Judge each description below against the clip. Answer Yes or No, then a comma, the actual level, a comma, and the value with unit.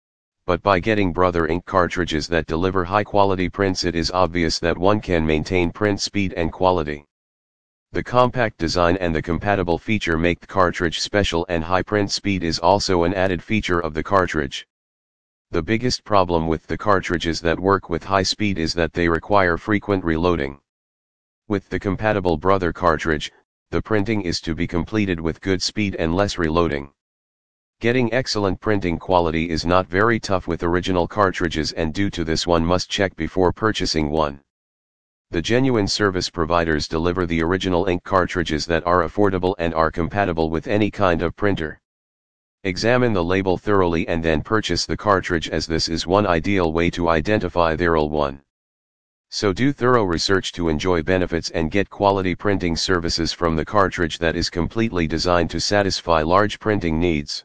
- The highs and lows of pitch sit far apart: No, average, 3.2 semitones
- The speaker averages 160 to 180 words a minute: Yes, average, 170 wpm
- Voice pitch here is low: Yes, very low, 90 Hz